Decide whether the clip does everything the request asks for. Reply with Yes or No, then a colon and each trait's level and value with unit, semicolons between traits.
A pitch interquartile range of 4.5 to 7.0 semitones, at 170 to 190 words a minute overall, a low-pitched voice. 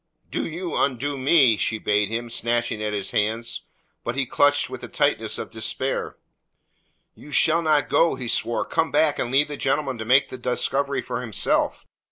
No: average, 3.9 semitones; average, 185 wpm; low, 130 Hz